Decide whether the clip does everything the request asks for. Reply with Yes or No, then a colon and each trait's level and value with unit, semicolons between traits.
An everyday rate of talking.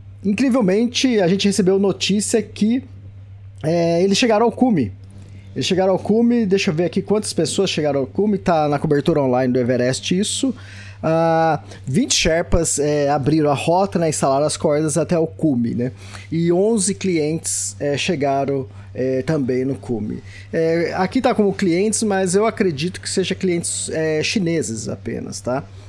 Yes: average, 160 wpm